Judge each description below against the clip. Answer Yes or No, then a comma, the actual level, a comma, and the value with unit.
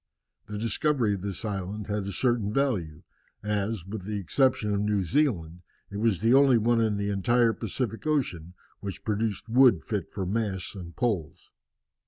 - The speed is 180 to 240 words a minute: No, average, 170 wpm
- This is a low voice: Yes, low, 105 Hz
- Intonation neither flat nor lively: Yes, average, 3.1 semitones